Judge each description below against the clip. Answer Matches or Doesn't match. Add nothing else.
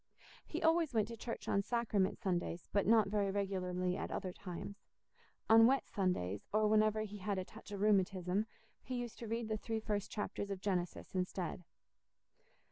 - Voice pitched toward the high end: Matches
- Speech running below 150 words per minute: Doesn't match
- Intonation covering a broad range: Doesn't match